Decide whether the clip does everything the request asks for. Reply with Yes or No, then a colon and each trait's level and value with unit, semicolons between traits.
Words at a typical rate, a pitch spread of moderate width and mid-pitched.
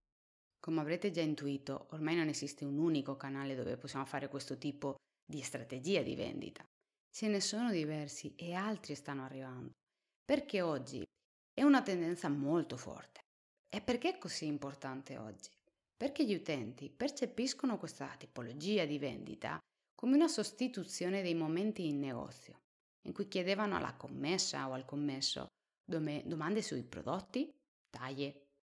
No: average, 140 wpm; wide, 6.4 semitones; medium, 155 Hz